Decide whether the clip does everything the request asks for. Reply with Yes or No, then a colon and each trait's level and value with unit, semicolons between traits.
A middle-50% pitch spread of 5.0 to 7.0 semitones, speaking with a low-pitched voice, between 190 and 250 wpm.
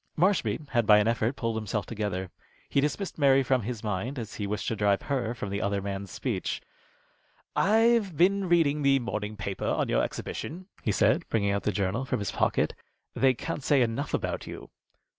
Yes: wide, 5.6 semitones; low, 115 Hz; average, 195 wpm